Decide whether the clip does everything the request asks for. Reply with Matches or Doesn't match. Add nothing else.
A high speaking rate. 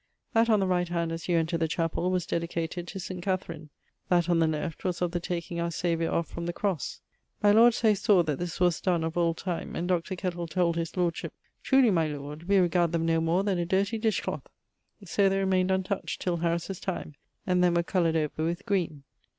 Matches